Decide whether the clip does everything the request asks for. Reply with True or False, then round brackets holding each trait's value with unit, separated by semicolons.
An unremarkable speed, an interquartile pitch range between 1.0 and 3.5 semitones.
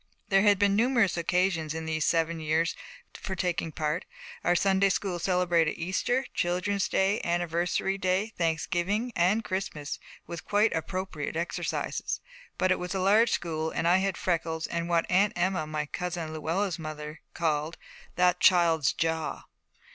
True (150 wpm; 2.9 semitones)